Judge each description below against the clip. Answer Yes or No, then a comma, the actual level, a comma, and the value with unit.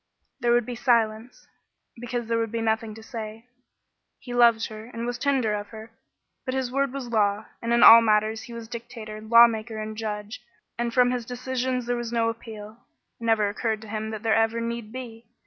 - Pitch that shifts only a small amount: Yes, narrow, 1.7 semitones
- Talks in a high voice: Yes, high, 230 Hz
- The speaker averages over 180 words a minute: Yes, average, 200 wpm